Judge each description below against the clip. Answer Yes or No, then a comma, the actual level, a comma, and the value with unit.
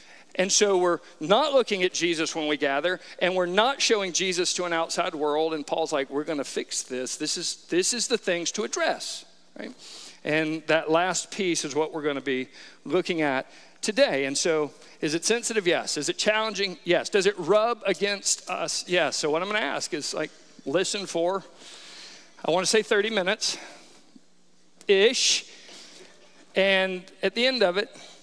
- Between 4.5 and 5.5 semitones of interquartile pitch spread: Yes, average, 4.9 semitones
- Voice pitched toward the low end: No, medium, 180 Hz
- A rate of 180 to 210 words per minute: Yes, average, 185 wpm